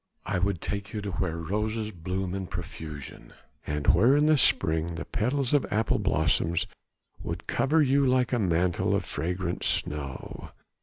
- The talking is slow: No, average, 160 wpm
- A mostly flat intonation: No, average, 5.2 semitones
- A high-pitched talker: No, very low, 95 Hz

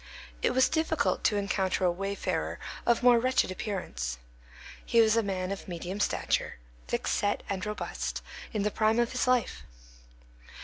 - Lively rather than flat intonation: No, average, 3.8 semitones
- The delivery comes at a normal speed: Yes, average, 145 wpm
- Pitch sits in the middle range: No, high, 210 Hz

